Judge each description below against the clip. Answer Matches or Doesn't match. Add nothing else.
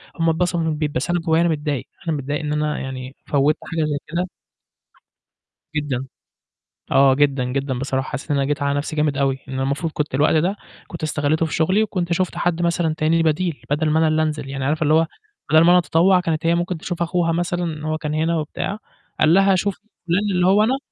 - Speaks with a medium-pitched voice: Matches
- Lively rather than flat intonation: Doesn't match